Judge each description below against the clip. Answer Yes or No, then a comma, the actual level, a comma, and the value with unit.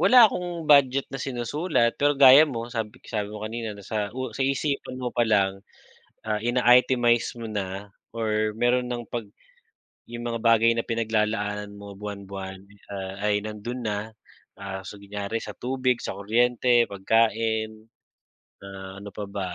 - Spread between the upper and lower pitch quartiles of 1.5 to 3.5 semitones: Yes, average, 3.1 semitones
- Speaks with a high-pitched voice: No, low, 115 Hz